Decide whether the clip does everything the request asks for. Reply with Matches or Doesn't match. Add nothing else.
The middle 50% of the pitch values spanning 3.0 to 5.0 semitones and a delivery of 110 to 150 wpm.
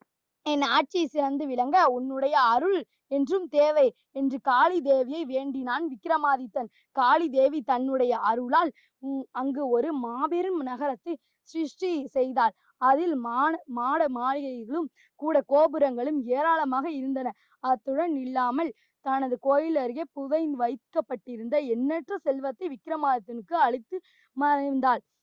Doesn't match